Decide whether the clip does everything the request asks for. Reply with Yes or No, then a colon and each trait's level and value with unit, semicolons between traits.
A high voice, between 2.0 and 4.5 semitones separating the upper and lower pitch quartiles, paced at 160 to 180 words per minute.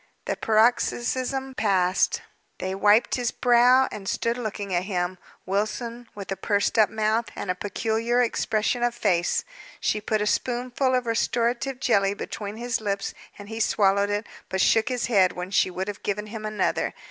Yes: high, 215 Hz; average, 3.2 semitones; average, 170 wpm